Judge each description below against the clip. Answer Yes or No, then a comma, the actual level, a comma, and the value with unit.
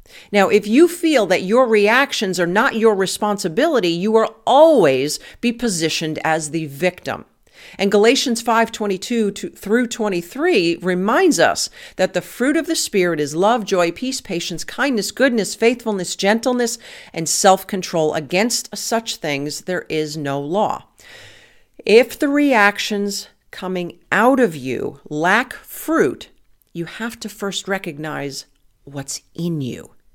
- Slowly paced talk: Yes, slow, 130 wpm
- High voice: Yes, high, 205 Hz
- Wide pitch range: Yes, wide, 5.7 semitones